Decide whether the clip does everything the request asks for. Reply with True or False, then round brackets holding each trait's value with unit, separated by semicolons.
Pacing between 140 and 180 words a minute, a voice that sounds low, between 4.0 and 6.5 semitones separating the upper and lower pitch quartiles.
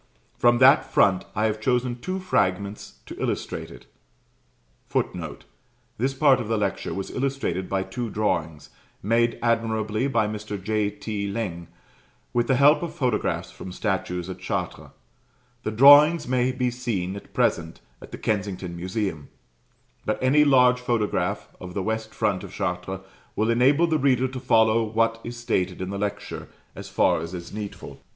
True (160 wpm; 110 Hz; 4.3 semitones)